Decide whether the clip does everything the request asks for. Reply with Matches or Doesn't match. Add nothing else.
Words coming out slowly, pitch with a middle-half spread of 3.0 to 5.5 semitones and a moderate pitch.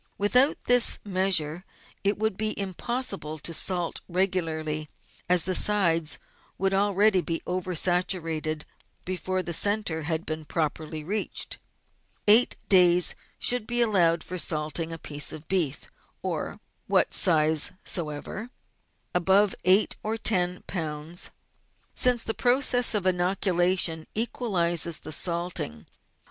Matches